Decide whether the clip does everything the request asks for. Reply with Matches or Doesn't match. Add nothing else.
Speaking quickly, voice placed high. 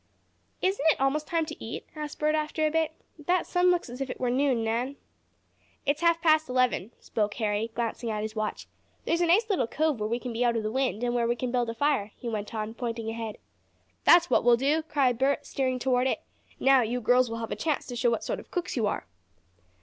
Matches